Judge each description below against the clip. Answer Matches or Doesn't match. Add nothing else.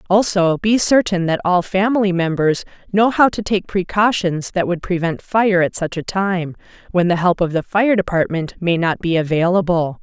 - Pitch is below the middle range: Doesn't match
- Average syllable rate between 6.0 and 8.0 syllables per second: Doesn't match